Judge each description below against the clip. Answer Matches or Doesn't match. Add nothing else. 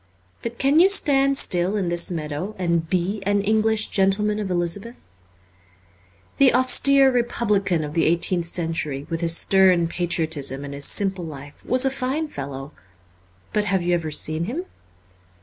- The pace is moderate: Matches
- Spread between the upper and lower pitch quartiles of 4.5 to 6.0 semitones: Matches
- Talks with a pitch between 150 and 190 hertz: Matches